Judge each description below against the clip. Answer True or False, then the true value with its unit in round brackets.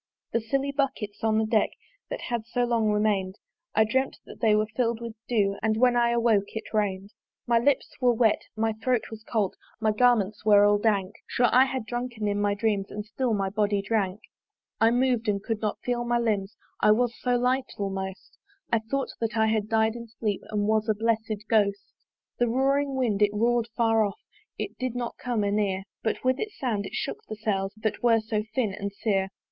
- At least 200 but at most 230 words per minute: True (205 wpm)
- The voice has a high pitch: True (220 Hz)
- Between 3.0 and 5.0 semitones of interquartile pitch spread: False (2.6 semitones)